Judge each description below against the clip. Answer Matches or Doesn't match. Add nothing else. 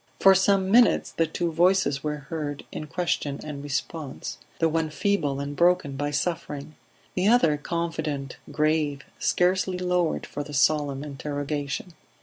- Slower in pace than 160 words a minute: Matches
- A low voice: Doesn't match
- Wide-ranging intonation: Doesn't match